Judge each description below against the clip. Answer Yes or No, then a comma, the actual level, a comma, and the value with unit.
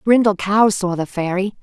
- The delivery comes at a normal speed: Yes, average, 185 wpm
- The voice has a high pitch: Yes, high, 195 Hz